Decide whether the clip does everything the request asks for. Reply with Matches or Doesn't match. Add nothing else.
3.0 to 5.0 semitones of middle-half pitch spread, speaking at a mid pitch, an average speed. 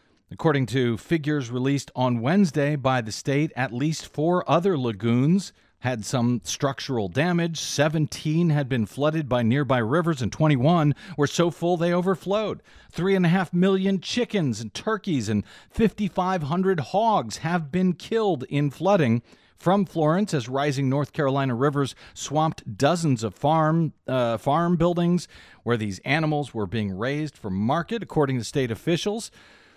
Doesn't match